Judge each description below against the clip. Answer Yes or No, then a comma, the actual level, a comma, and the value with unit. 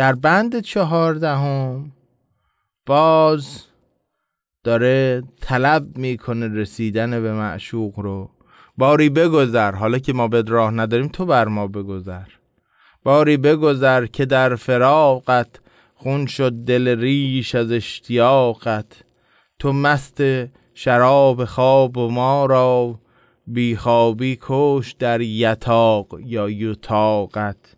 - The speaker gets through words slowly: Yes, slow, 105 wpm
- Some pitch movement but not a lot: Yes, average, 3.2 semitones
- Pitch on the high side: No, low, 125 Hz